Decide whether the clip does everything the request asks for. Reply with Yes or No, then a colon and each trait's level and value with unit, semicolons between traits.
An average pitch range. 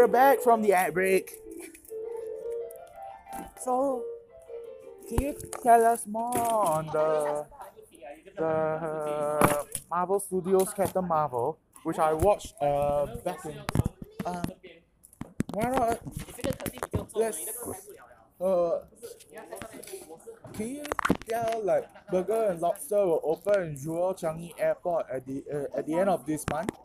No: wide, 7.9 semitones